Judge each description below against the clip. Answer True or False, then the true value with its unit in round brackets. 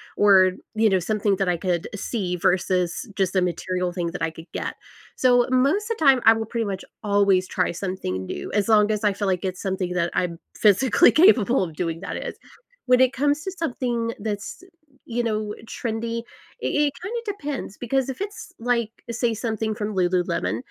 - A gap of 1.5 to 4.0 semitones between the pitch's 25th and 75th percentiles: False (5.0 semitones)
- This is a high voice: True (210 Hz)